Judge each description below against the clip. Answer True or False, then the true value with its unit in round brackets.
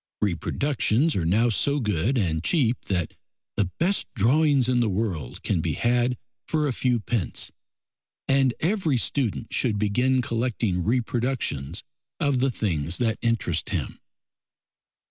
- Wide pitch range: False (4.6 semitones)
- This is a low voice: True (120 Hz)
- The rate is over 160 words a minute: False (135 wpm)